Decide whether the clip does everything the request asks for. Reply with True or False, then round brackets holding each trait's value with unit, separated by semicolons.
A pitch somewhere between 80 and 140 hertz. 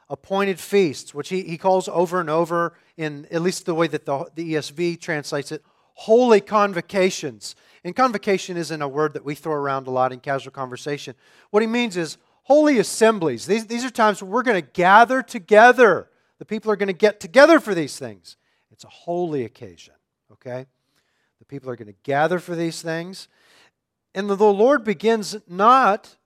False (175 Hz)